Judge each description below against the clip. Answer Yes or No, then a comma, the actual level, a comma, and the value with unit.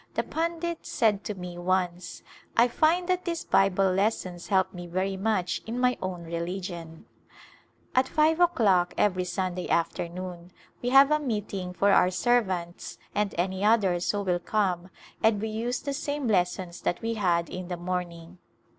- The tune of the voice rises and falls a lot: No, average, 4.4 semitones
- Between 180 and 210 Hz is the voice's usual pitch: Yes, high, 190 Hz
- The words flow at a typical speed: Yes, average, 170 wpm